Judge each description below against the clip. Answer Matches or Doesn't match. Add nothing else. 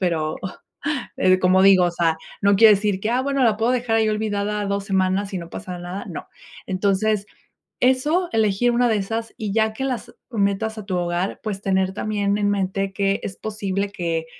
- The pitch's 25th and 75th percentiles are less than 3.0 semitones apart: Matches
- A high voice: Matches